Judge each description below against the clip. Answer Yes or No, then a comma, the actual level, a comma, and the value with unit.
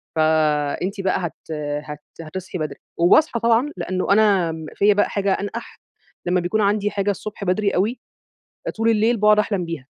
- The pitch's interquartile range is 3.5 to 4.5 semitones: Yes, average, 3.8 semitones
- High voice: Yes, high, 195 Hz